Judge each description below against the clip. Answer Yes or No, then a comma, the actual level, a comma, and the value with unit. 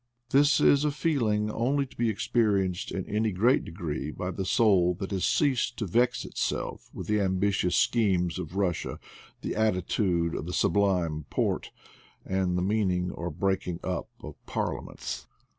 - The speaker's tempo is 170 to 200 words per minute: No, average, 160 wpm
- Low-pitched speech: Yes, very low, 95 Hz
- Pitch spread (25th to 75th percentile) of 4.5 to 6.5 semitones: No, average, 3.8 semitones